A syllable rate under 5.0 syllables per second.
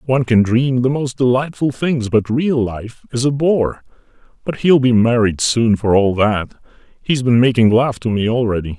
Yes: 4.7 syllables/s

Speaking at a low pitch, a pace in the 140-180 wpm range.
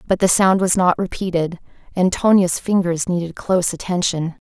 No: medium, 180 Hz; average, 160 wpm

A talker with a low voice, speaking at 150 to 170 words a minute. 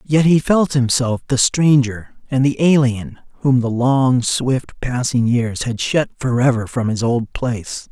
Yes: low, 125 Hz; average, 165 wpm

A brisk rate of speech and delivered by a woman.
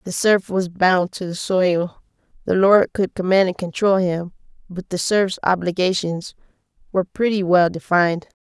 No: average, 155 wpm; female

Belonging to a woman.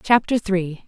Yes: female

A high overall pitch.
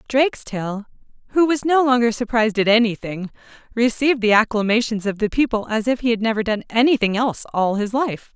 Yes: high, 230 Hz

